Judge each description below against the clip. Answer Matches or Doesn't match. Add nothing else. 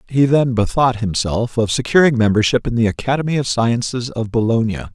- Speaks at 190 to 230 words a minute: Doesn't match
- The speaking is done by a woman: Doesn't match